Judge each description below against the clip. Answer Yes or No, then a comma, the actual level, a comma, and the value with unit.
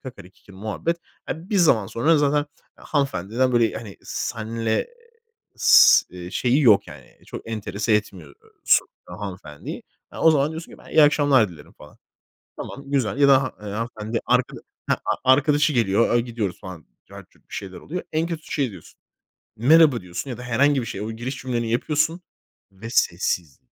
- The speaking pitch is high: No, low, 120 Hz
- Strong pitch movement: Yes, wide, 6.0 semitones